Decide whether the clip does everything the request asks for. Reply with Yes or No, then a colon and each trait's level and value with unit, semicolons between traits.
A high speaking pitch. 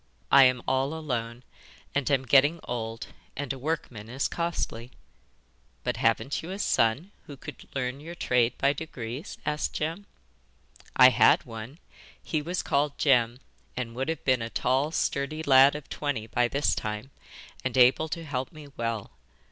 No: low, 135 Hz